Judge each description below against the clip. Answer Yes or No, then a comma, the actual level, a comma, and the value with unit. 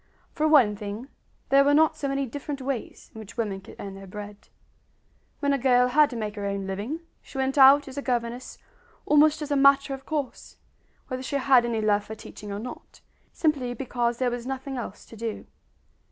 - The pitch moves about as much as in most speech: Yes, average, 4.1 semitones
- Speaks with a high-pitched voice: Yes, very high, 255 Hz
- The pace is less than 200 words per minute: No, fast, 205 wpm